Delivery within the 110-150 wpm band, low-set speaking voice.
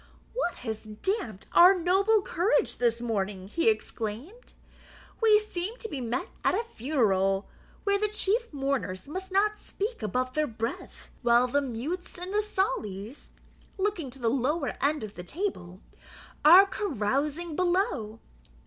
No: average, 145 wpm; very high, 295 Hz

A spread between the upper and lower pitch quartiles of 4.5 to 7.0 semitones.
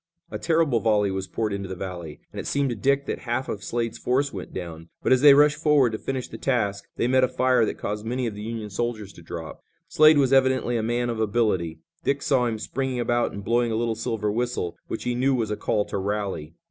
No: average, 4.1 semitones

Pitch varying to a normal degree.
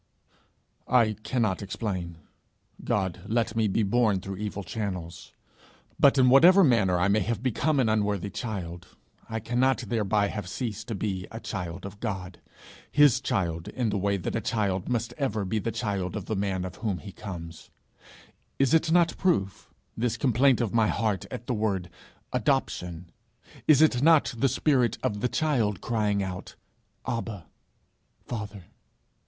Yes: average, 4.1 semitones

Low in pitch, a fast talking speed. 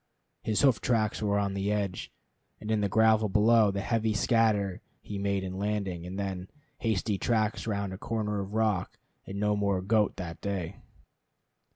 No: low, 100 Hz; average, 175 wpm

